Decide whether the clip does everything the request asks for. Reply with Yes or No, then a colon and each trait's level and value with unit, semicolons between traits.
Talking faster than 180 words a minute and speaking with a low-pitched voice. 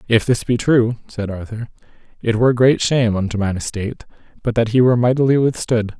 Yes: average, 190 wpm; low, 115 Hz